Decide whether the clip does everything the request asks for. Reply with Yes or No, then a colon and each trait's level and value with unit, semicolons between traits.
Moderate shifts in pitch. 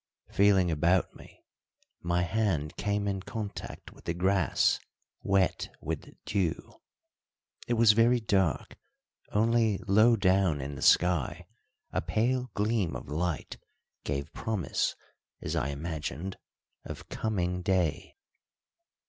Yes: average, 4.1 semitones